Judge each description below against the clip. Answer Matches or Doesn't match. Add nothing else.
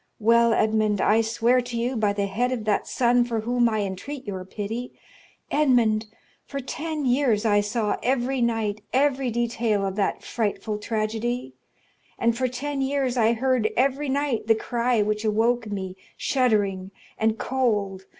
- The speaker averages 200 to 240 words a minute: Doesn't match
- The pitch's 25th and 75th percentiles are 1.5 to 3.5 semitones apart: Matches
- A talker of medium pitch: Doesn't match